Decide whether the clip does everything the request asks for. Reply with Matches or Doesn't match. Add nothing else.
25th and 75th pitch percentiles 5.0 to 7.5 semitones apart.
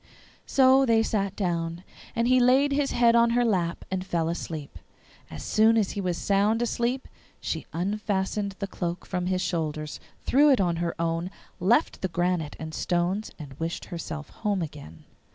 Matches